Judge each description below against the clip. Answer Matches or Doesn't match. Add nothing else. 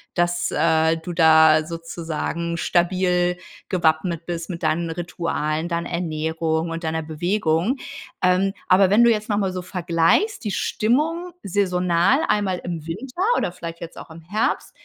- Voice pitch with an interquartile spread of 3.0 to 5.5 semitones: Doesn't match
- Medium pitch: Matches